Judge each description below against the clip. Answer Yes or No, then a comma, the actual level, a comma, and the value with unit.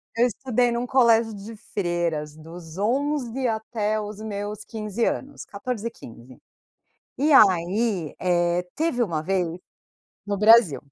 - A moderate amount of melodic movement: Yes, average, 5.0 semitones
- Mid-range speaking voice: No, high, 210 Hz